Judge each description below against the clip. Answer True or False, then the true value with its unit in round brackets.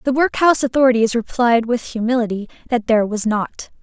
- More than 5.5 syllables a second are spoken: True (5.9 syllables/s)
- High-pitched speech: True (235 Hz)